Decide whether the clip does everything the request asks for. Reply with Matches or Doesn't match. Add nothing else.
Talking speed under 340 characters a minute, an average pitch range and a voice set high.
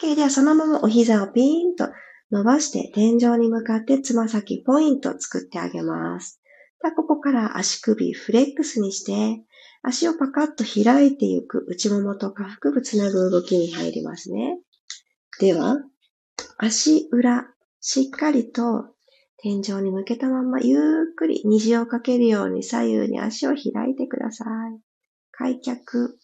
Matches